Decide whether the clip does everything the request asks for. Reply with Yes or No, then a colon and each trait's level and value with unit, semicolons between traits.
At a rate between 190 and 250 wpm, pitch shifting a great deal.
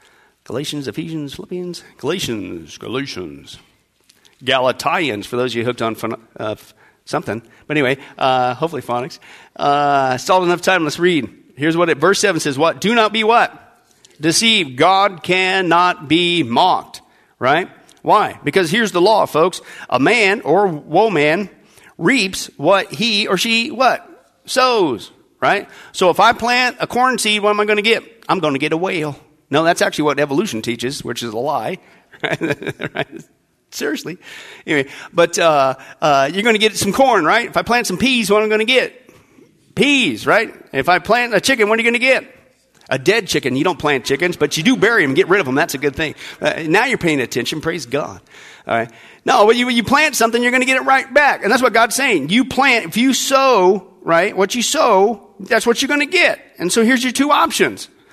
Yes: fast, 205 wpm; wide, 7.5 semitones